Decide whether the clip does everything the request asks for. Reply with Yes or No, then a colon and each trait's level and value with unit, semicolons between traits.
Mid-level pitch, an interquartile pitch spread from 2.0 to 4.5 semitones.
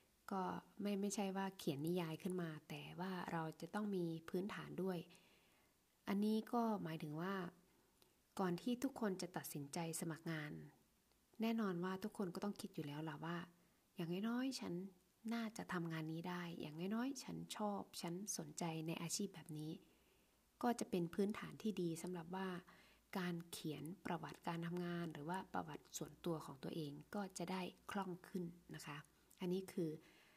Yes: medium, 180 Hz; average, 3.1 semitones